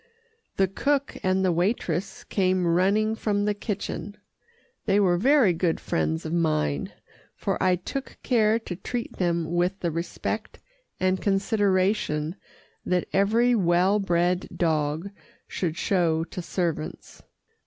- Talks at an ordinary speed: No, slow, 130 wpm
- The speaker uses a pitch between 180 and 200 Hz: Yes, medium, 185 Hz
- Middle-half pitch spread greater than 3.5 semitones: No, average, 3.1 semitones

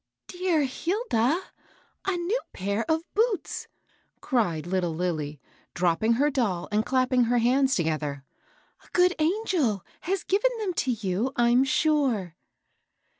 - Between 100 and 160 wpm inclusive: Yes, average, 155 wpm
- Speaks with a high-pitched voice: Yes, very high, 250 Hz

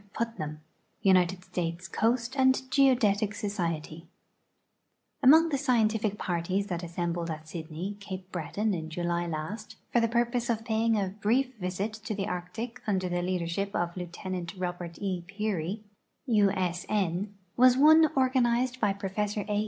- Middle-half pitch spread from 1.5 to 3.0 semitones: No, average, 4.6 semitones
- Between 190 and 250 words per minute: No, average, 145 wpm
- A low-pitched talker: No, high, 200 Hz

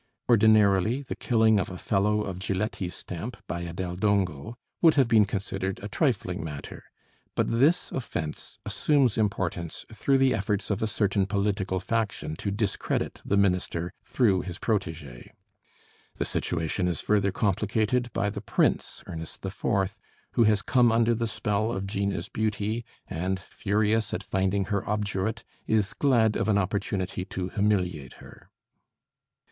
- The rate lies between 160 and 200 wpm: No, average, 150 wpm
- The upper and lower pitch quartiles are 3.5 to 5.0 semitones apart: No, average, 2.8 semitones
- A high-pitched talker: No, low, 100 Hz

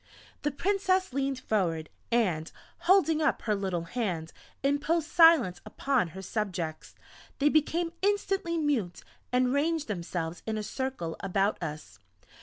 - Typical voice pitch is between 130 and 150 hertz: No, very high, 250 Hz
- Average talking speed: No, slow, 130 wpm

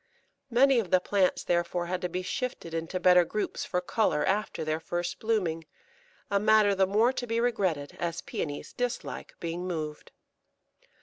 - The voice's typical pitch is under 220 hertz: Yes, medium, 185 Hz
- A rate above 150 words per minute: Yes, average, 165 wpm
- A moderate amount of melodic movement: Yes, average, 4.2 semitones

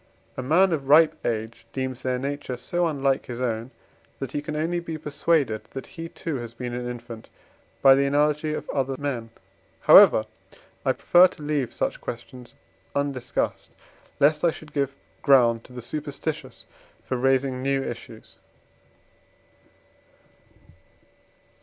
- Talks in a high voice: No, low, 135 Hz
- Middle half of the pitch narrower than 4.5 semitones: Yes, average, 3.4 semitones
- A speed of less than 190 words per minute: Yes, average, 140 wpm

